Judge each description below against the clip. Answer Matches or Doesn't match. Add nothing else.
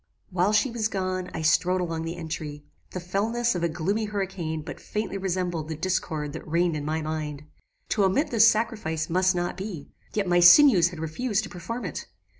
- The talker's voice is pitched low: Doesn't match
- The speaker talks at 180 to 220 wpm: Matches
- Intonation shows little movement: Doesn't match